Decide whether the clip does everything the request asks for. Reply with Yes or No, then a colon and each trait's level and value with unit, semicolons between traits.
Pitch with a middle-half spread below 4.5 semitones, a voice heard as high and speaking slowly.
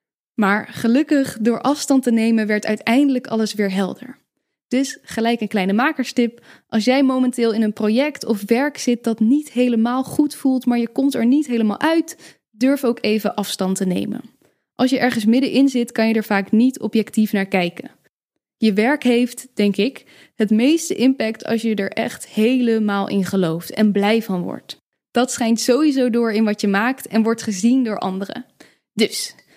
No: average, 3.1 semitones; high, 230 Hz; average, 180 wpm